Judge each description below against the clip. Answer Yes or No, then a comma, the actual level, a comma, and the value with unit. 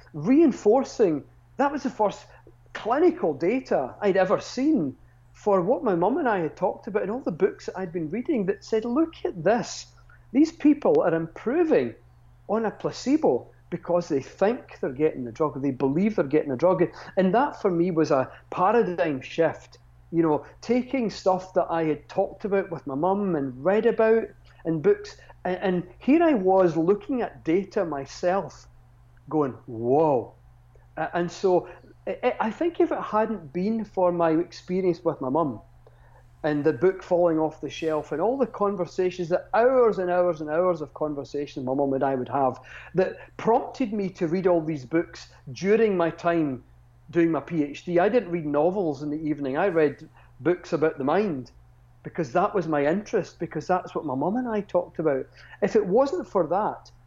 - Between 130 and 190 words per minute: Yes, average, 185 wpm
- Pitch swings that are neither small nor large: No, wide, 5.8 semitones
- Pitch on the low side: No, medium, 175 Hz